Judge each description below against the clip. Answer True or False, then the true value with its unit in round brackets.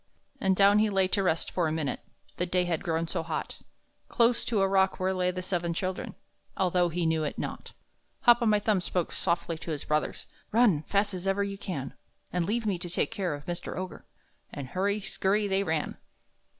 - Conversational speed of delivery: False (215 wpm)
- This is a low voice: False (185 Hz)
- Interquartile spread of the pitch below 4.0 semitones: True (2.9 semitones)